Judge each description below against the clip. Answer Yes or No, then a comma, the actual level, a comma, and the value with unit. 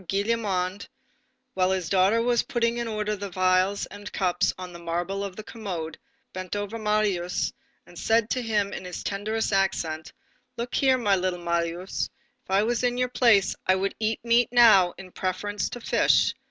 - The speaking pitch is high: Yes, high, 200 Hz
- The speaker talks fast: No, average, 180 wpm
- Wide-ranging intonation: No, average, 3.4 semitones